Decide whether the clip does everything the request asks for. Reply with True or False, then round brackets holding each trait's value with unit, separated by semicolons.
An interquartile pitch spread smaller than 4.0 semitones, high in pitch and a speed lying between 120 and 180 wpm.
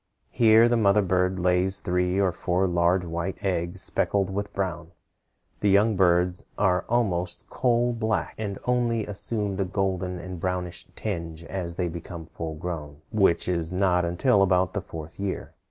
False (2.4 semitones; 90 Hz; 160 wpm)